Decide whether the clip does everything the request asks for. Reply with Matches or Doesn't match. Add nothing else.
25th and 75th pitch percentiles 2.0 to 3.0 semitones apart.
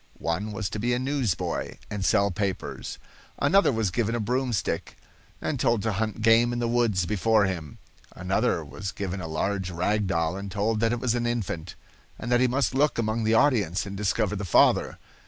Doesn't match